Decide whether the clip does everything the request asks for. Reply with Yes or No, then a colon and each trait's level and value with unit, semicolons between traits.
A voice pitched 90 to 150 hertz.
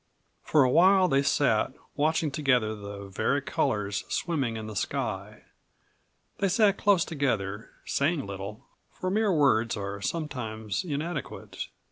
Yes: low, 135 Hz